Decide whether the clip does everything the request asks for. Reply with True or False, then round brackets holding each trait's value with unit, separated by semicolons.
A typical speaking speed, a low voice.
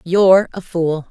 False (165 wpm; 175 Hz)